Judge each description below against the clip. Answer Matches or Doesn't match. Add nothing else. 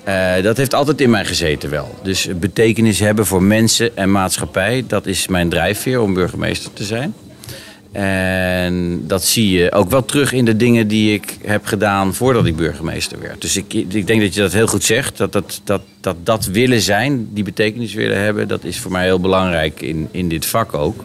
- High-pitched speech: Doesn't match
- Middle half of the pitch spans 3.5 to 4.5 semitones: Doesn't match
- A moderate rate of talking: Doesn't match